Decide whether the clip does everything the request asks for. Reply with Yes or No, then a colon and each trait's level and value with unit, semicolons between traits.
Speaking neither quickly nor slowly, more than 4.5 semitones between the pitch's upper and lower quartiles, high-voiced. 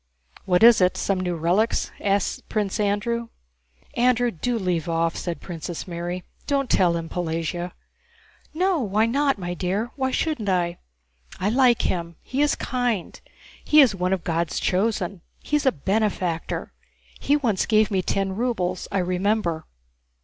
Yes: average, 150 wpm; average, 4.9 semitones; high, 195 Hz